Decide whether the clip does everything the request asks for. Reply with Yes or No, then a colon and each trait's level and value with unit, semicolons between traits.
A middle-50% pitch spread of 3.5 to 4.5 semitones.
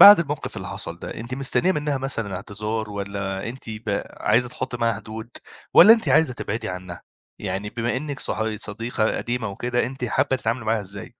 Yes: average, 3.8 semitones